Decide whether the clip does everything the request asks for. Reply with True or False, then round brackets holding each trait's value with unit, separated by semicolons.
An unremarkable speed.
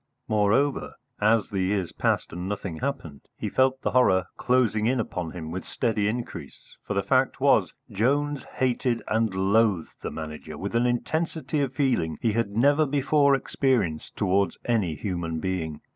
True (160 wpm)